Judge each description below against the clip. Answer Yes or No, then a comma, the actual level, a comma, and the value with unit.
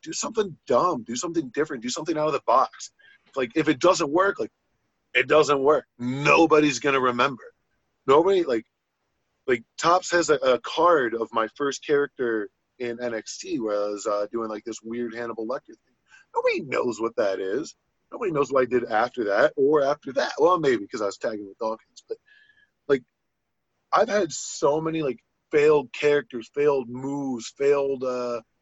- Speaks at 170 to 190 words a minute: Yes, average, 180 wpm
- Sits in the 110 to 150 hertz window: Yes, medium, 140 Hz